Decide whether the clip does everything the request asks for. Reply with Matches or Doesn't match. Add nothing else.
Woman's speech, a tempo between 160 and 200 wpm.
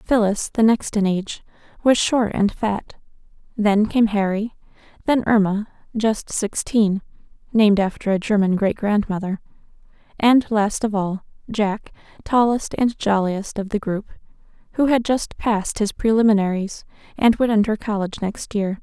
Doesn't match